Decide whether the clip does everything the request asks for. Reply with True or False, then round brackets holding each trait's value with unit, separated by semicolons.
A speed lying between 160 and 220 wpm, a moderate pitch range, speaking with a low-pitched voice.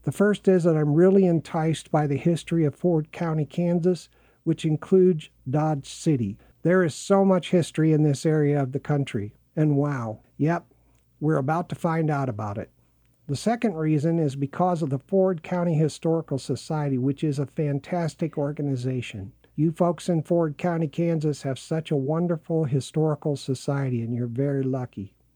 False (170 wpm; 3.4 semitones; 155 Hz)